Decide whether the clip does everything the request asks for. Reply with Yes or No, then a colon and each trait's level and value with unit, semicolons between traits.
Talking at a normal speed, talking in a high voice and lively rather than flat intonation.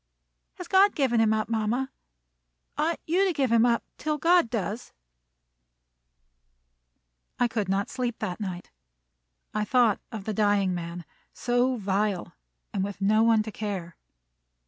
No: average, 145 wpm; high, 220 Hz; average, 3.9 semitones